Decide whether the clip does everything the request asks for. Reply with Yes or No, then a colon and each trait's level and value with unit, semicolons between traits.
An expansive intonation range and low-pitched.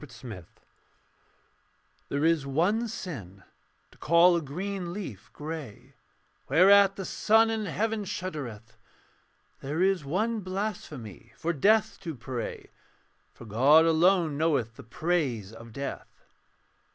No: wide, 7.1 semitones; medium, 160 Hz